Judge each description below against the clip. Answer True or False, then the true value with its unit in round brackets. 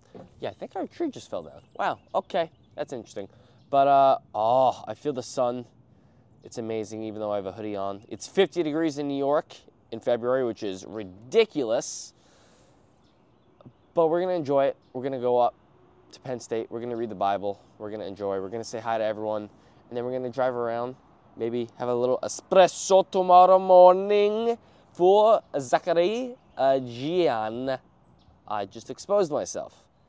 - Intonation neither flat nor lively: False (6.8 semitones)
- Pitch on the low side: True (125 Hz)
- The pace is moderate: True (170 wpm)